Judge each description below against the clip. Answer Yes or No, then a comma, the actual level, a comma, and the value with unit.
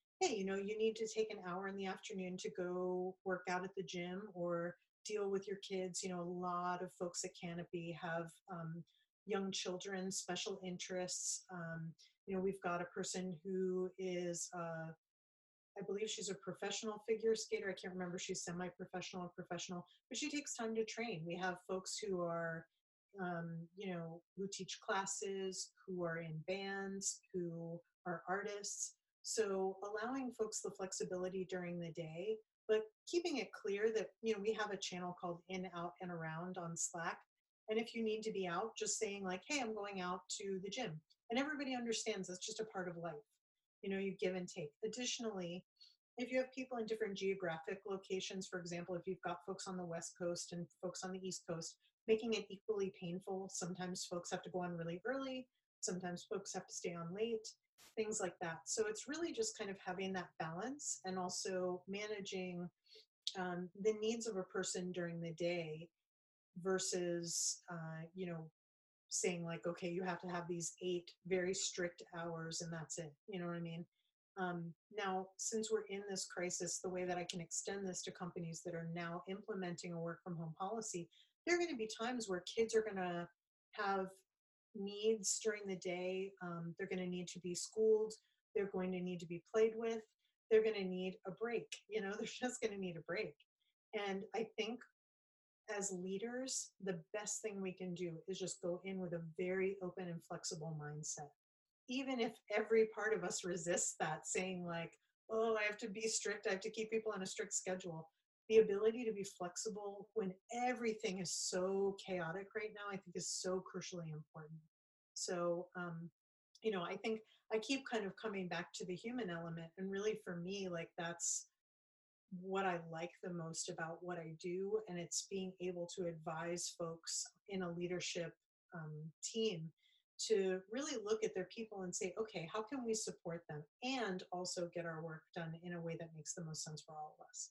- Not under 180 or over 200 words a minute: Yes, average, 195 wpm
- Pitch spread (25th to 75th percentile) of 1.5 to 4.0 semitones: Yes, average, 3.4 semitones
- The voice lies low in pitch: No, medium, 185 Hz